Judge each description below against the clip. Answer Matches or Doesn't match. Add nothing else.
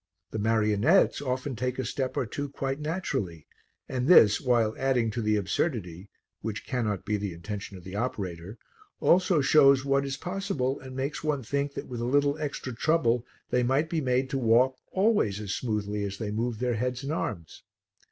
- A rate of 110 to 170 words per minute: Doesn't match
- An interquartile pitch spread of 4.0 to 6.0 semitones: Matches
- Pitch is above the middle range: Doesn't match